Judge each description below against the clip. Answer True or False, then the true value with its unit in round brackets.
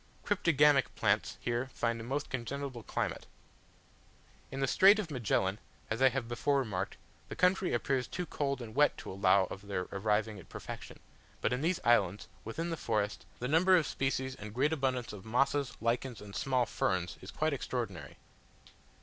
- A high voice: False (125 Hz)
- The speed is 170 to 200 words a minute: True (175 wpm)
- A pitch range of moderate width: True (4.6 semitones)